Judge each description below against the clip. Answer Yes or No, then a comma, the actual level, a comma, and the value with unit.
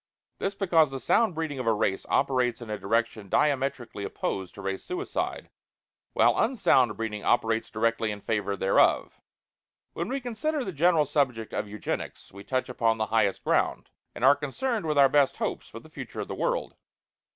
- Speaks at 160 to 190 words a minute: Yes, average, 180 wpm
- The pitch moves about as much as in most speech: No, wide, 6.3 semitones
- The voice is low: Yes, low, 125 Hz